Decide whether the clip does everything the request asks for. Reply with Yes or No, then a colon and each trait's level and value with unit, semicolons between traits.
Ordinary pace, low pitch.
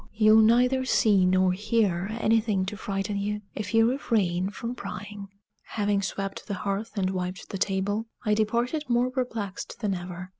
No: average, 160 wpm; high, 205 Hz